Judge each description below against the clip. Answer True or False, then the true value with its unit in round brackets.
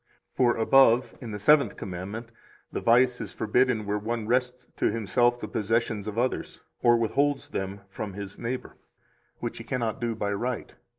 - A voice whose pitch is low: True (115 Hz)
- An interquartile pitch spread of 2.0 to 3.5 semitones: True (2.9 semitones)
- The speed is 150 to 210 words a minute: True (170 wpm)